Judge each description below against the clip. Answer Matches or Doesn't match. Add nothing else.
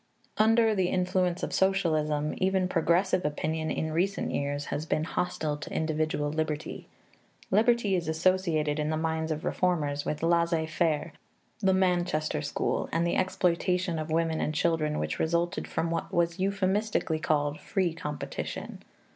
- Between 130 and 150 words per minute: Matches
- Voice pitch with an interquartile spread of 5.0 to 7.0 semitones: Doesn't match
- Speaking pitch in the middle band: Matches